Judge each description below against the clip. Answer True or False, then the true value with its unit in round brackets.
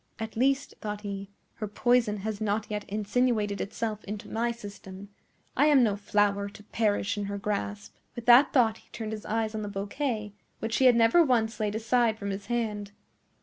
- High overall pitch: True (215 Hz)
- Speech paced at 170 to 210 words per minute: True (190 wpm)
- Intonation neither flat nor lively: False (2.3 semitones)